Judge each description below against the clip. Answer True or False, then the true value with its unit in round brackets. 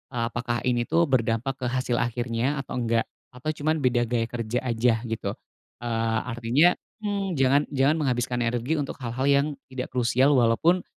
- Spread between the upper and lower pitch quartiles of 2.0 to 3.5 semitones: True (2.8 semitones)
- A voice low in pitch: True (125 Hz)